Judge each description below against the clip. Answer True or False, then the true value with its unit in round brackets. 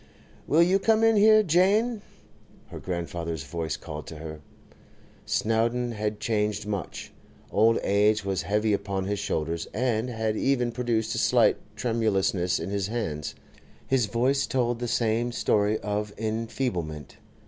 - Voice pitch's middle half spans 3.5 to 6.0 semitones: True (4.0 semitones)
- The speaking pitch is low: True (110 Hz)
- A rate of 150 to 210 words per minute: False (140 wpm)